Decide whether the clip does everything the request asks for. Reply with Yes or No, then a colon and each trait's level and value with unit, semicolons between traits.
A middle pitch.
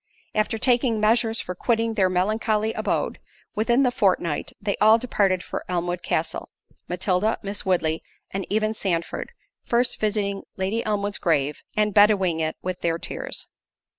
No: high, 205 Hz